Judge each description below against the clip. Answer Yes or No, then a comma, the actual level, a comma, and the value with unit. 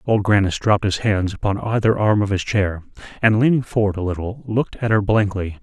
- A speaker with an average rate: No, fast, 215 wpm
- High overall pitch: No, low, 105 Hz